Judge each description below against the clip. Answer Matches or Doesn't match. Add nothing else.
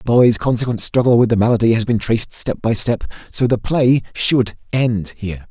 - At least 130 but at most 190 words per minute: Doesn't match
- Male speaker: Matches